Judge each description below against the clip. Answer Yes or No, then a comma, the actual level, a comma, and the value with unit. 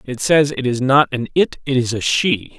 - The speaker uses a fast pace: Yes, fast, 255 wpm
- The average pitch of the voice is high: No, low, 130 Hz